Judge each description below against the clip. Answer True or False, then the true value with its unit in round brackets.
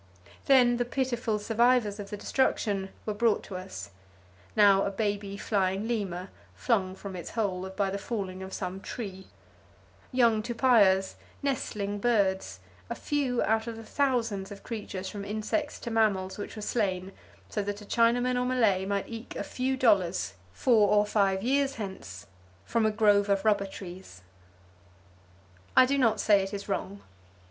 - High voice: True (205 Hz)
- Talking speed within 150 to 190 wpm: True (160 wpm)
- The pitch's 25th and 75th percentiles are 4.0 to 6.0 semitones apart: False (3.4 semitones)